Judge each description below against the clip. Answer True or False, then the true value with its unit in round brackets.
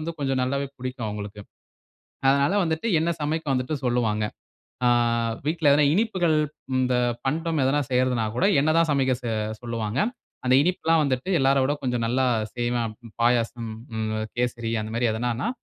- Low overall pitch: True (130 Hz)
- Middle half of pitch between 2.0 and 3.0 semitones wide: False (3.9 semitones)